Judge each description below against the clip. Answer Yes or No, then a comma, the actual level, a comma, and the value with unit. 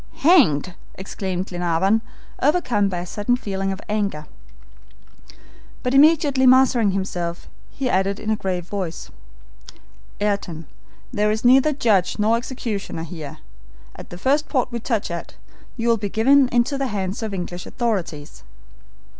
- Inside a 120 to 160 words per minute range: Yes, average, 145 wpm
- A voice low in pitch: No, high, 210 Hz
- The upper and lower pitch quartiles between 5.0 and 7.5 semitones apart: Yes, average, 5.3 semitones